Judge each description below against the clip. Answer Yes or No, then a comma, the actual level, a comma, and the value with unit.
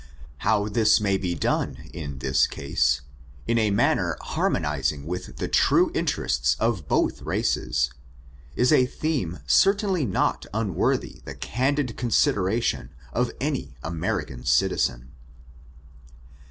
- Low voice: Yes, low, 100 Hz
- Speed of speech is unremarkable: No, slow, 115 wpm